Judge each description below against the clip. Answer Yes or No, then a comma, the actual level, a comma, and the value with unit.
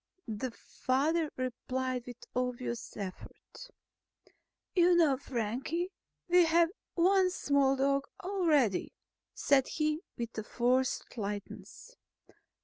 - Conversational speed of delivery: No, slow, 95 wpm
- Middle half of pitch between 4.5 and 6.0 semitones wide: Yes, average, 5.3 semitones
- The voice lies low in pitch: No, very high, 270 Hz